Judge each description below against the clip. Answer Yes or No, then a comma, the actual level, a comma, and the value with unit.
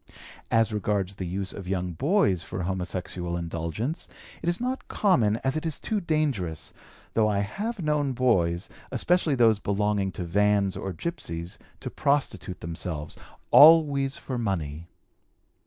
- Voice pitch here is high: No, low, 105 Hz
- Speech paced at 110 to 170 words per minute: Yes, average, 140 wpm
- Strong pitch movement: Yes, wide, 7.9 semitones